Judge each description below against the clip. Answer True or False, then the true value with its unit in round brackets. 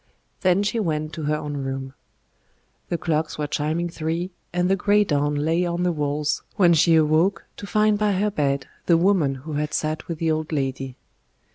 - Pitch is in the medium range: True (160 Hz)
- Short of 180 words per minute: False (190 wpm)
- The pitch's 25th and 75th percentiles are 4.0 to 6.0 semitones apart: False (3.3 semitones)